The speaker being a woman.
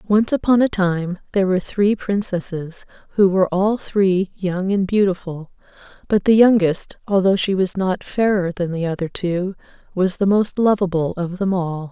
Yes: female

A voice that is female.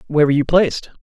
No: male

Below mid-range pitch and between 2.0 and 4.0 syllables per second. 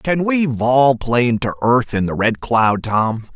Yes: low, 125 Hz; 3.8 syllables/s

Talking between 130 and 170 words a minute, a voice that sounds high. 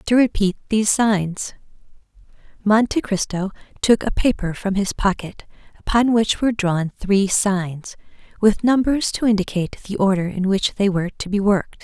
Yes: average, 155 wpm; high, 205 Hz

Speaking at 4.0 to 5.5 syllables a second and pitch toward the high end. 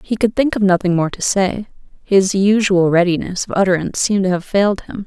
No: 5.8 syllables/s; high, 195 Hz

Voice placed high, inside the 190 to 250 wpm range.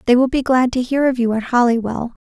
No: high, 245 Hz; fast, 270 wpm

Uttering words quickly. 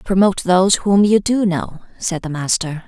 No: average, 190 wpm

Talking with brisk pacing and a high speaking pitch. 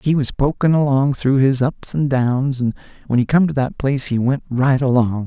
No: fast, 230 wpm; low, 135 Hz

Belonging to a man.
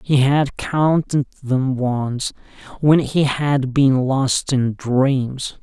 Yes: male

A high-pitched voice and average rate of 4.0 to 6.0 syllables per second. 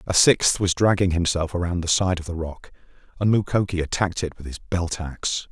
No: very low, 90 Hz; 5.3 syllables/s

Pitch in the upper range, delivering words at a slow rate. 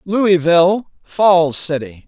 No: medium, 175 Hz; slow, 85 wpm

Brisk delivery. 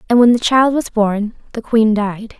Yes: fast, 225 wpm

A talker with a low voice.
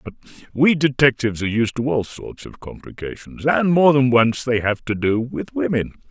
Yes: low, 125 Hz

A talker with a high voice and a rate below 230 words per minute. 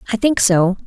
Yes: high, 210 Hz; fast, 210 wpm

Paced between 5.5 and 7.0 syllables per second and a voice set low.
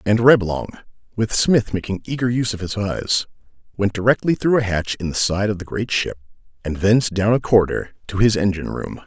Yes: 5.7 syllables/s; low, 105 Hz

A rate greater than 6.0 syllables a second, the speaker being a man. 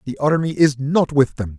No: 4.8 syllables/s; male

